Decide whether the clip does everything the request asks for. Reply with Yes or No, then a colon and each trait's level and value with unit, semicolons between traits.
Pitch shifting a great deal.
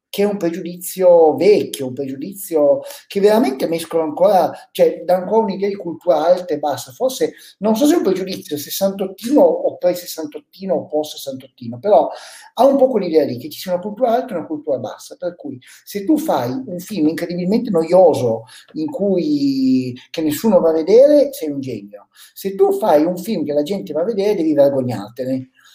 Yes: wide, 6.5 semitones